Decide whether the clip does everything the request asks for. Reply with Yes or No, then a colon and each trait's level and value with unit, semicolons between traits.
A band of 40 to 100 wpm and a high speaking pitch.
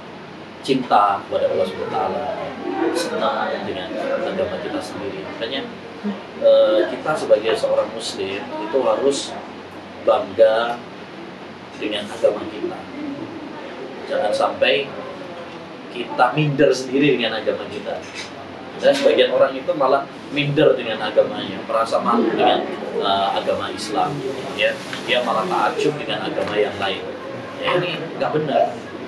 No: average, 115 wpm; very high, 275 Hz